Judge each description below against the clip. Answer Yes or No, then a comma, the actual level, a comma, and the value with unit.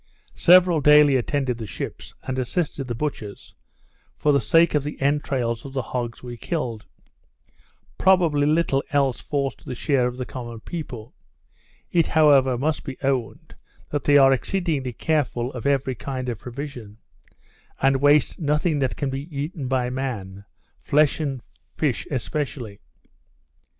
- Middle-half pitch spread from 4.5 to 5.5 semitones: No, average, 3.1 semitones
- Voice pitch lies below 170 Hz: Yes, low, 135 Hz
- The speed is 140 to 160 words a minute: Yes, average, 150 wpm